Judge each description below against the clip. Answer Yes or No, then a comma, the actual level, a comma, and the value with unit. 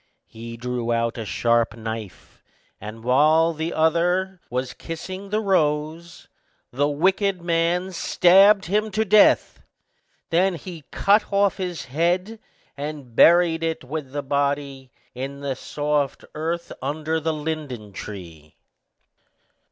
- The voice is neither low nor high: Yes, medium, 155 Hz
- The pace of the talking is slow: Yes, slow, 125 wpm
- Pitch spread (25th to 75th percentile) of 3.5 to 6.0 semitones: Yes, wide, 5.4 semitones